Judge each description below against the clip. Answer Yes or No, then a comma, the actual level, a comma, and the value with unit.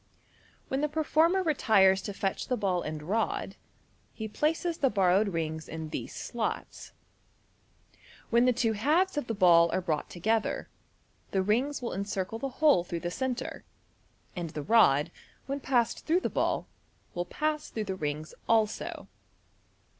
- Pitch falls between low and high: No, high, 215 Hz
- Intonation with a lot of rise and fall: Yes, wide, 7.2 semitones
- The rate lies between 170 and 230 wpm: No, average, 155 wpm